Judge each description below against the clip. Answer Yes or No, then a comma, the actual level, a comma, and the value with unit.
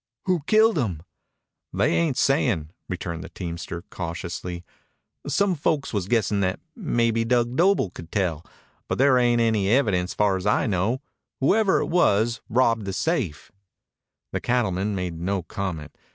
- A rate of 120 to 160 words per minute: Yes, average, 150 wpm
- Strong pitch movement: Yes, wide, 5.9 semitones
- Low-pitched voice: Yes, low, 105 Hz